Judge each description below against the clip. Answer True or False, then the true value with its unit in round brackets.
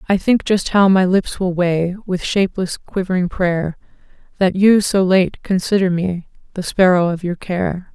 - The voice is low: False (185 Hz)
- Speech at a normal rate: True (175 wpm)